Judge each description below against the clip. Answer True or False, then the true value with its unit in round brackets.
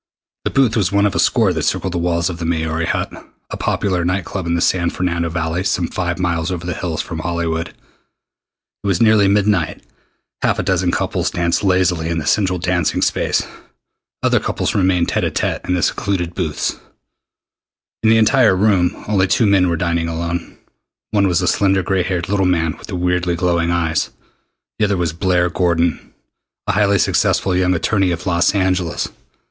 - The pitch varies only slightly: True (2.2 semitones)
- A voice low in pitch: True (90 Hz)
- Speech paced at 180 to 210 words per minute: True (190 wpm)